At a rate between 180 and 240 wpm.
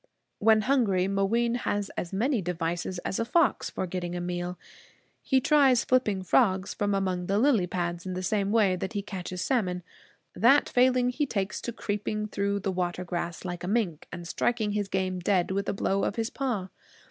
Yes: average, 195 wpm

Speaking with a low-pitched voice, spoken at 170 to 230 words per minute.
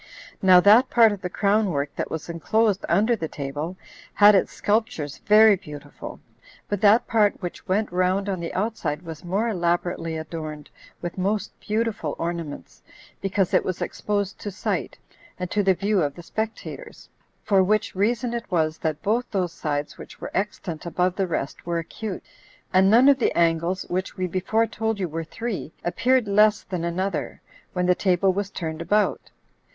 No: high, 190 Hz; average, 175 wpm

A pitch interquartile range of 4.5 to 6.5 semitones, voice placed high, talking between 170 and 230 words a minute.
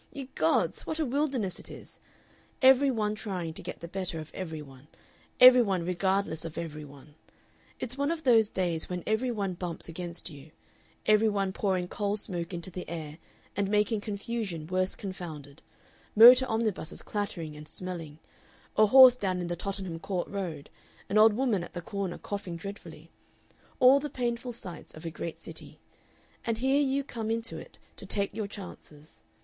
Yes: average, 5.0 semitones; high, 195 Hz; average, 175 wpm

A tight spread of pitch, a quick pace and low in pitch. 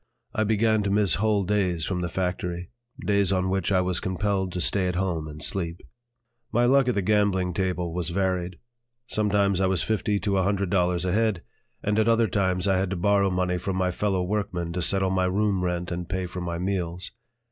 Yes: narrow, 2.2 semitones; fast, 210 wpm; very low, 95 Hz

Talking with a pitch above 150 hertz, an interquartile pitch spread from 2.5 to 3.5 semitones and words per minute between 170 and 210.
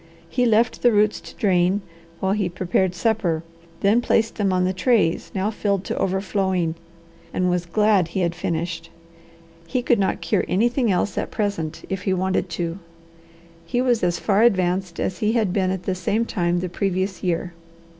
Yes: high, 190 Hz; average, 3.1 semitones; average, 180 wpm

